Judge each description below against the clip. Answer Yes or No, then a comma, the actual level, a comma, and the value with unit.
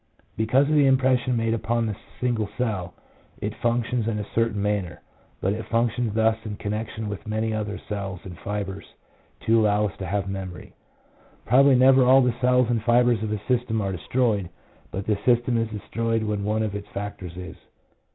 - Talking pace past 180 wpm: Yes, average, 190 wpm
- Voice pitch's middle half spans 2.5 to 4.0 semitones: Yes, average, 2.9 semitones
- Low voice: Yes, low, 110 Hz